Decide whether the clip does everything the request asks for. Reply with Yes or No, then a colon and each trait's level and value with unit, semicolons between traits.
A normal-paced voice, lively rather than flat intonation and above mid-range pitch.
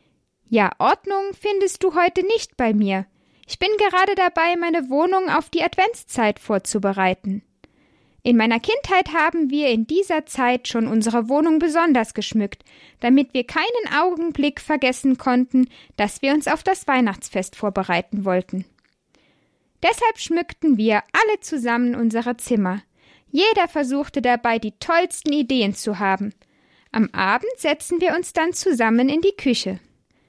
Yes: average, 140 wpm; wide, 7.4 semitones; very high, 280 Hz